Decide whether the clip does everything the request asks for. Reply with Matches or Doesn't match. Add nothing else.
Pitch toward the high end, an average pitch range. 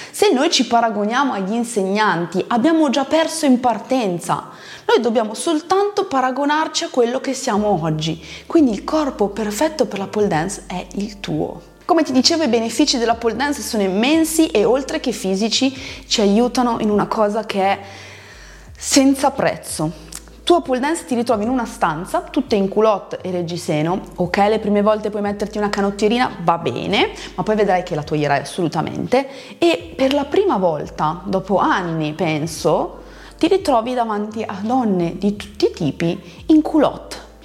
Doesn't match